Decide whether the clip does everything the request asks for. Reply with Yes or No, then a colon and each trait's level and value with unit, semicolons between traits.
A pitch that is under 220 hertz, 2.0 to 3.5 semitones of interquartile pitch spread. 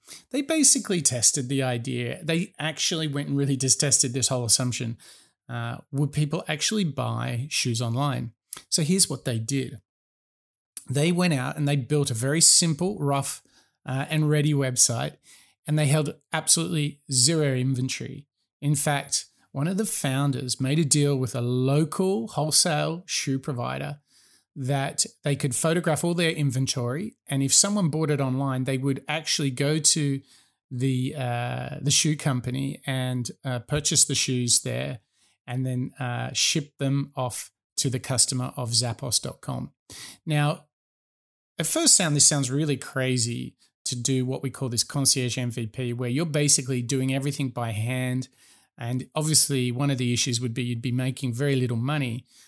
Yes: low, 135 Hz; average, 2.9 semitones